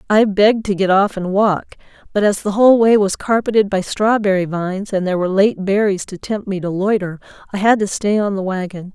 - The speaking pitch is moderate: No, high, 200 Hz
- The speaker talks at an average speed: No, fast, 230 wpm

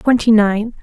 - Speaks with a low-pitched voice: No, high, 220 Hz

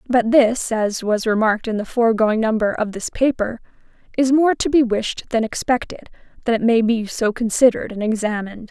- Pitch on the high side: Yes, high, 230 Hz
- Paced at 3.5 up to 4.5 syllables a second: Yes, 3.9 syllables/s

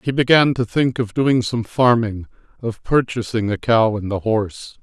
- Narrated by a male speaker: Yes, male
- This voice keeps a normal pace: Yes, average, 185 wpm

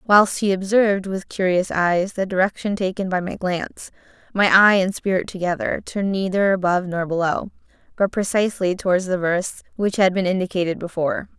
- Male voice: No, female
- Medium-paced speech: Yes, average, 170 wpm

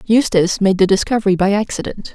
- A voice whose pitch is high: Yes, high, 200 Hz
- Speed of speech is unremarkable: Yes, average, 170 wpm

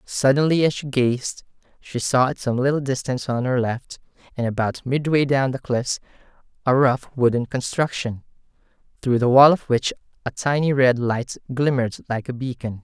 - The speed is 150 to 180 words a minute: Yes, average, 170 wpm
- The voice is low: Yes, low, 130 Hz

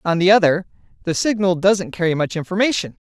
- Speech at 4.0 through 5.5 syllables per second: No, 6.0 syllables/s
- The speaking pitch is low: No, medium, 185 Hz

